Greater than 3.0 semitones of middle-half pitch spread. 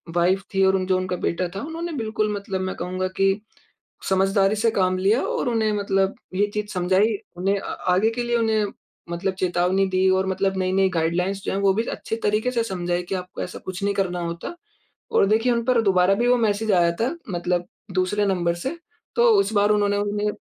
No: narrow, 2.5 semitones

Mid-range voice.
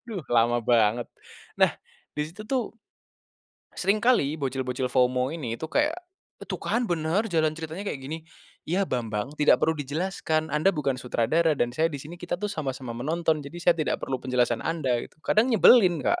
Yes: medium, 155 Hz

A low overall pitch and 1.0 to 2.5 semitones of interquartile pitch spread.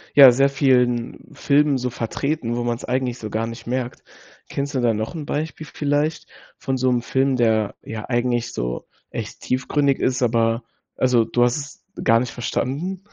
No: low, 125 Hz; average, 2.9 semitones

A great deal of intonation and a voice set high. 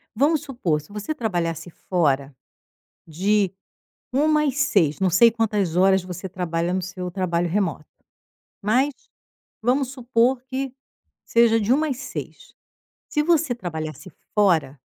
Yes: wide, 6.8 semitones; high, 205 Hz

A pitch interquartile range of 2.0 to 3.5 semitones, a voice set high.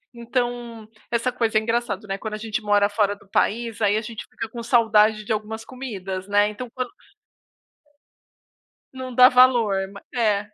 Yes: narrow, 2.5 semitones; high, 220 Hz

